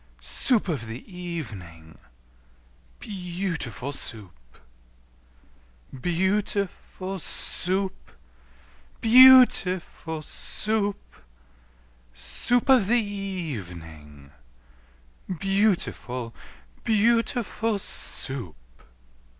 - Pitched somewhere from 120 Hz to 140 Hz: No, medium, 180 Hz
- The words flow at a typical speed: No, slow, 75 wpm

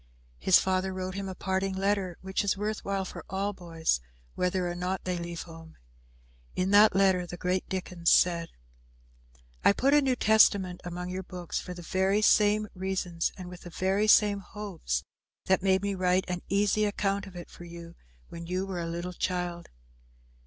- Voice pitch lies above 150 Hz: Yes, medium, 185 Hz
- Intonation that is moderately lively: No, narrow, 1.9 semitones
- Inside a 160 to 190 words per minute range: Yes, average, 185 wpm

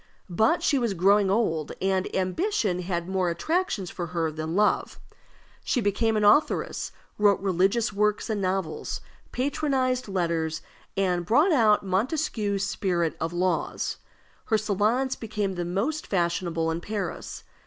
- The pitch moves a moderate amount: Yes, average, 4.1 semitones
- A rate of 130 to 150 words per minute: Yes, slow, 135 wpm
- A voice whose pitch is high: Yes, high, 195 Hz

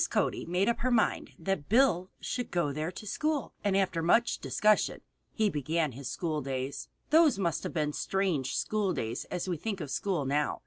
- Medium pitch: Yes, medium, 180 Hz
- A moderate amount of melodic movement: No, wide, 6.1 semitones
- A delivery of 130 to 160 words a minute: No, average, 190 wpm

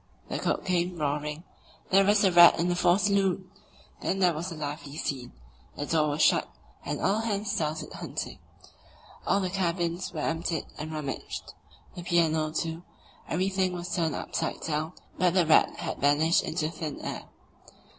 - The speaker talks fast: No, average, 165 wpm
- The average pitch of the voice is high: No, medium, 170 Hz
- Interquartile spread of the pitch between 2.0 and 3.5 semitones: Yes, average, 3.0 semitones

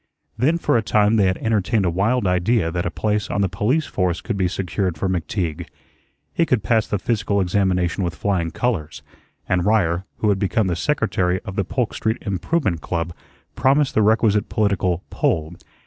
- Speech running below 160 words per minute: No, average, 185 wpm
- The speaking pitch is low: Yes, low, 100 Hz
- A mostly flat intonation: No, average, 3.7 semitones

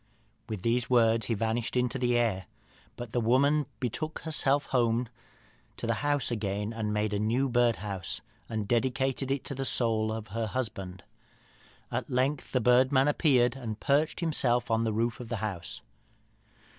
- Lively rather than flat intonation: No, average, 3.1 semitones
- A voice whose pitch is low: Yes, low, 120 Hz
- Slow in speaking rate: No, average, 165 wpm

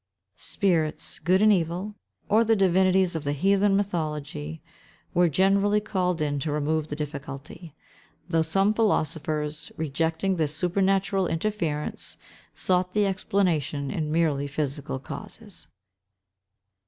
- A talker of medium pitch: Yes, medium, 170 Hz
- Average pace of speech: No, slow, 115 wpm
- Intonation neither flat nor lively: Yes, average, 4.3 semitones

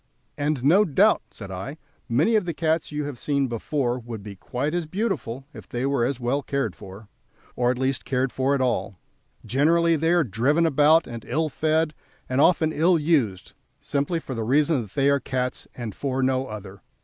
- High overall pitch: No, medium, 140 Hz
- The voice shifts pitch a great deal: No, average, 4.5 semitones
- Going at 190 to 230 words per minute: Yes, average, 195 wpm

